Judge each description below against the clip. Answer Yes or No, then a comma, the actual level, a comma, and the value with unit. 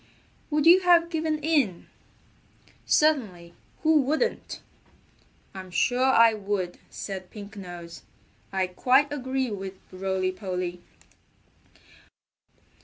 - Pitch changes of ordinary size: No, wide, 7.8 semitones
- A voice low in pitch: No, high, 210 Hz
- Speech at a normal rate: No, slow, 100 wpm